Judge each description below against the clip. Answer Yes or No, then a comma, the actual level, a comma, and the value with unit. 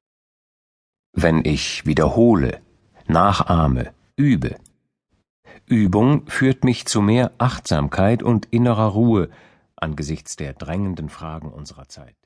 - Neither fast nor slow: No, slow, 100 wpm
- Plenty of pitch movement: Yes, wide, 7.2 semitones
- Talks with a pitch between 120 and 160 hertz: No, very low, 95 Hz